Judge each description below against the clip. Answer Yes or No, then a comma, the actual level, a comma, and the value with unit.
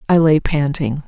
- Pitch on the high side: No, medium, 150 Hz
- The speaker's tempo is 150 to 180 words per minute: Yes, average, 170 wpm